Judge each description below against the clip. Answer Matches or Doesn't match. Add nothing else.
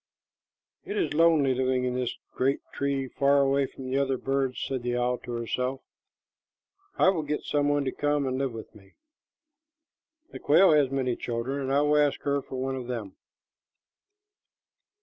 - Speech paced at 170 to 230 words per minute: Matches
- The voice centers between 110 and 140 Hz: Matches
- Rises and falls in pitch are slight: Matches